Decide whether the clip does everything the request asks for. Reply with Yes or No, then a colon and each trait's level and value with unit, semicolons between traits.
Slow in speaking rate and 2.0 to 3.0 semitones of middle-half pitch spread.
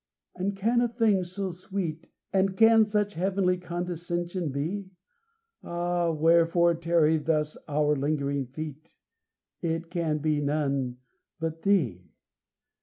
No: slow, 115 wpm; average, 3.7 semitones